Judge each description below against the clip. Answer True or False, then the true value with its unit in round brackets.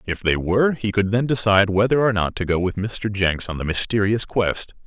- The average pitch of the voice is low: True (100 Hz)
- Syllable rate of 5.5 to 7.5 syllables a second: False (5.3 syllables/s)